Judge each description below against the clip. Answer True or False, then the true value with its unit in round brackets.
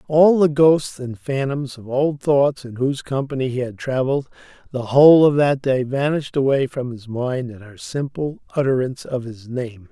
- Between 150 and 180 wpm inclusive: False (190 wpm)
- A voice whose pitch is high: False (135 Hz)